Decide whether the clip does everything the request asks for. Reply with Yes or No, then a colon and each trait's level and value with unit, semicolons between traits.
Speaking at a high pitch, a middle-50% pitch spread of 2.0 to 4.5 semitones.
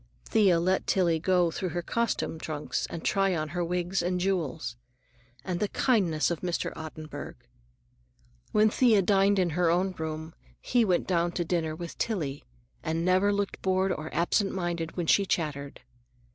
No: medium, 175 Hz; average, 2.9 semitones